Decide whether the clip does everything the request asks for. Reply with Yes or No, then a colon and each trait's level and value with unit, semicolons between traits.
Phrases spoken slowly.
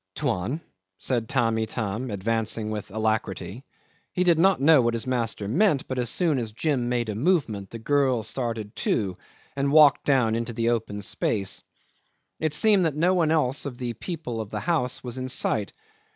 No: average, 180 wpm